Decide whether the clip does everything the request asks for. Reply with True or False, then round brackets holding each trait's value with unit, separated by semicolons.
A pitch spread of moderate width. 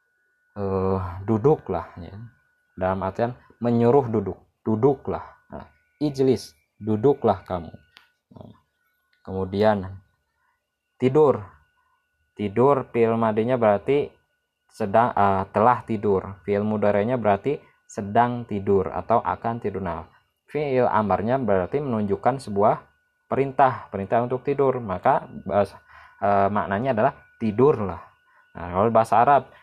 False (6.0 semitones)